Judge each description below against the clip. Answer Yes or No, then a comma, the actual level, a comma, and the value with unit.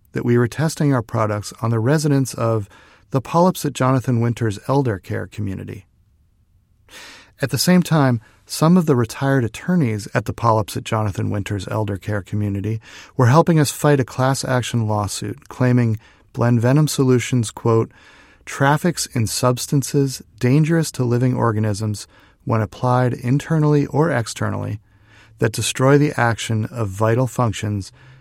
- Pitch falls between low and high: No, low, 120 Hz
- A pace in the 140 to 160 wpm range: Yes, average, 145 wpm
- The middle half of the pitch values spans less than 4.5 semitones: Yes, average, 4.1 semitones